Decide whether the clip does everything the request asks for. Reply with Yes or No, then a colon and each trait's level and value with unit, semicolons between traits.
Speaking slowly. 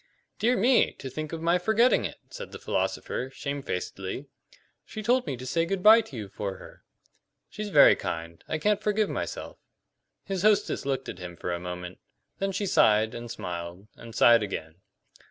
No: average, 180 wpm